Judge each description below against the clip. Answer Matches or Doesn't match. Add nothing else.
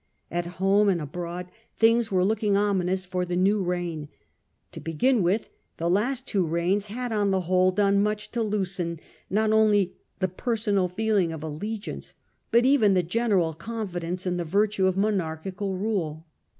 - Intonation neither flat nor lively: Matches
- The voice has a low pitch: Doesn't match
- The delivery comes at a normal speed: Matches